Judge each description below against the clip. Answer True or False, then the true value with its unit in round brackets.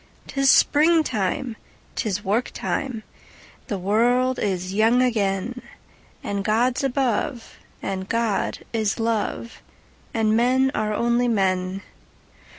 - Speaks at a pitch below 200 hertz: False (225 Hz)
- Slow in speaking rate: True (90 wpm)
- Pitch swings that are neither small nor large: True (3.7 semitones)